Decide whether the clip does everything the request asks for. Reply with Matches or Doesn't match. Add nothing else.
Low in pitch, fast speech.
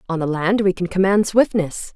Doesn't match